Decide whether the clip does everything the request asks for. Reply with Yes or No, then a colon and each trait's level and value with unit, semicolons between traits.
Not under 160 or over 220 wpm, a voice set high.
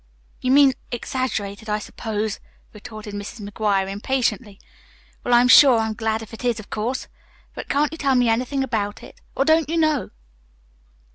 Yes: average, 165 wpm; high, 230 Hz